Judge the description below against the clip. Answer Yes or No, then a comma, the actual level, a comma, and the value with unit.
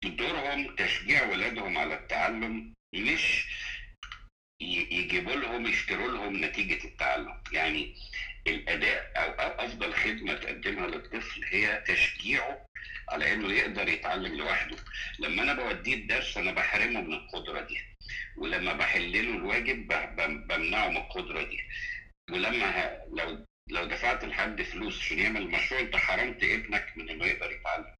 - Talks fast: No, average, 125 wpm